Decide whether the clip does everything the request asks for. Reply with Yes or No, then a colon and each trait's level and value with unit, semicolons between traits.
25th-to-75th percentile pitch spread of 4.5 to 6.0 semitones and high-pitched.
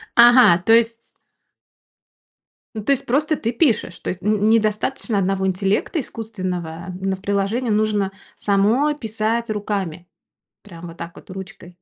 No: average, 3.4 semitones; high, 210 Hz